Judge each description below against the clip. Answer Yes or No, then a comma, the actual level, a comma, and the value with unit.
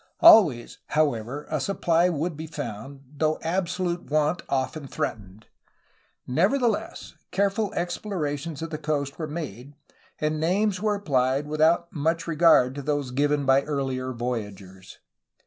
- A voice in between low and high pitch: Yes, medium, 150 Hz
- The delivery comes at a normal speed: No, slow, 130 wpm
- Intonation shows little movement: No, average, 4.2 semitones